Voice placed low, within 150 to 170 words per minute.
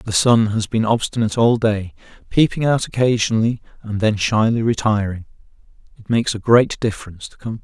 Yes: low, 110 Hz; average, 165 wpm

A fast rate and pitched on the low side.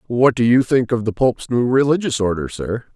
Yes: fast, 225 wpm; low, 120 Hz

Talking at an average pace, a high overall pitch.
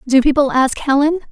Yes: average, 185 wpm; very high, 275 Hz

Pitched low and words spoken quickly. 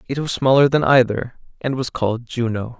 No: low, 125 Hz; average, 195 wpm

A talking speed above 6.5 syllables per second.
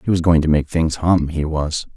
No: 5.0 syllables/s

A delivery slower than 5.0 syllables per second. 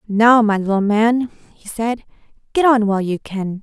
Yes: 4.6 syllables/s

